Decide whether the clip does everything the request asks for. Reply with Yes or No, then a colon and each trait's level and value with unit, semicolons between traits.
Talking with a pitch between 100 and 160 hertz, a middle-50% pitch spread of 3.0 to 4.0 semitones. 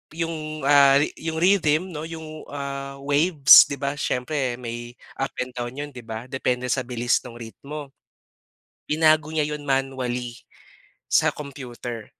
Yes: medium, 140 Hz; average, 3.7 semitones